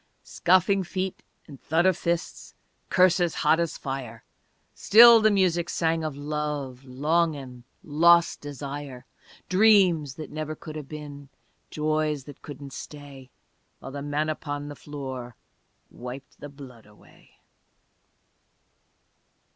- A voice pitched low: No, medium, 150 Hz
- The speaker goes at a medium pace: No, slow, 120 wpm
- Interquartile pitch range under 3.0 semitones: No, average, 3.6 semitones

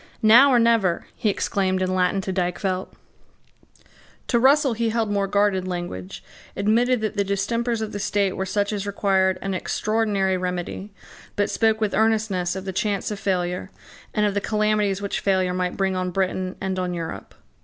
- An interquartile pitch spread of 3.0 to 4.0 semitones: No, narrow, 2.5 semitones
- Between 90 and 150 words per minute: No, average, 175 wpm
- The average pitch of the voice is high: Yes, high, 195 Hz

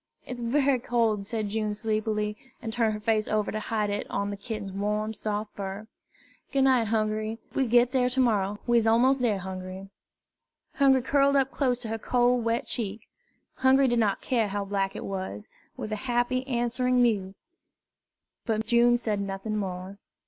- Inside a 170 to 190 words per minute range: Yes, average, 180 wpm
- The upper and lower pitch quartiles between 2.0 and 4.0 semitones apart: Yes, average, 2.9 semitones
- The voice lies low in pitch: No, high, 220 Hz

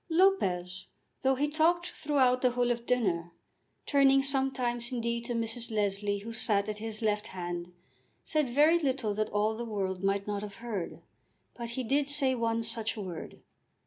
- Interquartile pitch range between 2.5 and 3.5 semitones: No, average, 4.3 semitones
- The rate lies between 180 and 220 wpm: No, average, 170 wpm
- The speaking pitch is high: Yes, high, 230 Hz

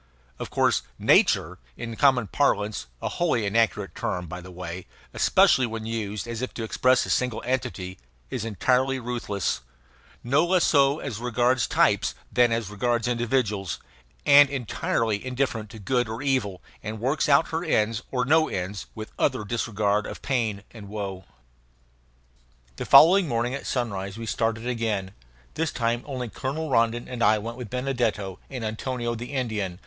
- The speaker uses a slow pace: No, average, 160 wpm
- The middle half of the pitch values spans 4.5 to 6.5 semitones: No, average, 3.6 semitones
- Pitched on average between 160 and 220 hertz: No, low, 115 Hz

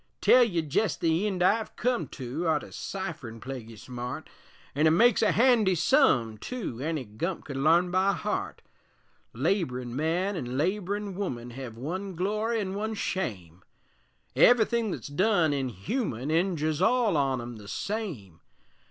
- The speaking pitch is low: No, medium, 170 Hz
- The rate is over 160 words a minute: No, average, 145 wpm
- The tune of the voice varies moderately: No, wide, 7.9 semitones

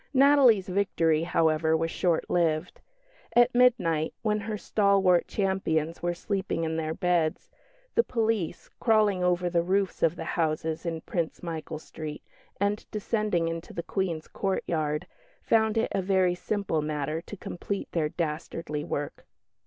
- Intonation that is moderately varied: Yes, average, 4.0 semitones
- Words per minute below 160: Yes, average, 145 wpm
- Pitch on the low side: No, medium, 175 Hz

